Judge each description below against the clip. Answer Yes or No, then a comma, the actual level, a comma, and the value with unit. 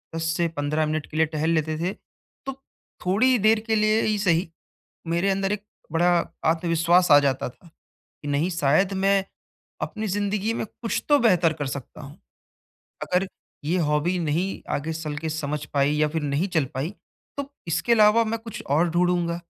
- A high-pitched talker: No, medium, 170 Hz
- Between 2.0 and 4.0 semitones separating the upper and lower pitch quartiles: No, average, 4.5 semitones